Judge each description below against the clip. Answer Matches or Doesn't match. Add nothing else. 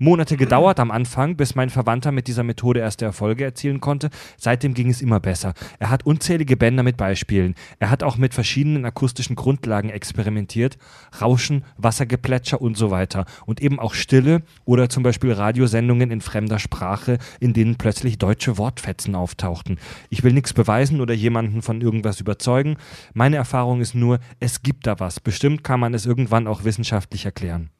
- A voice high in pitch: Doesn't match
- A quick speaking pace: Doesn't match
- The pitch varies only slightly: Doesn't match